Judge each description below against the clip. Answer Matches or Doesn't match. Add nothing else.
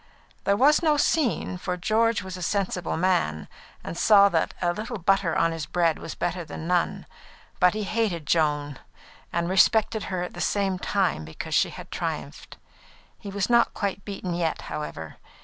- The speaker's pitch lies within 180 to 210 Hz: Matches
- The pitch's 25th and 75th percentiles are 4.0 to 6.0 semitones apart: Doesn't match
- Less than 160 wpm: Doesn't match